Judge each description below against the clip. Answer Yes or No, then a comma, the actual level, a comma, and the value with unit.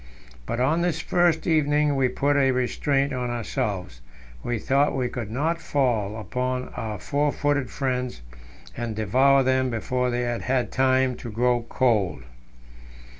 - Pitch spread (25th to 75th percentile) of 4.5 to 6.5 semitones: No, average, 2.8 semitones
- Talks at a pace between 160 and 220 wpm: No, average, 150 wpm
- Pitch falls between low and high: No, low, 130 Hz